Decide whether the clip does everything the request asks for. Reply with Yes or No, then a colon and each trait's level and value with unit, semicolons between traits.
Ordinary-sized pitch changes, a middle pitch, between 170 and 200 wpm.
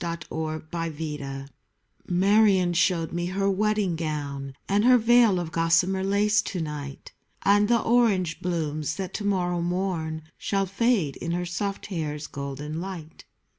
No: average, 3.9 semitones; medium, 175 Hz; average, 145 wpm